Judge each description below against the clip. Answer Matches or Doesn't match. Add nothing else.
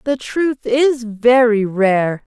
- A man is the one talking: Doesn't match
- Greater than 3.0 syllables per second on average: Doesn't match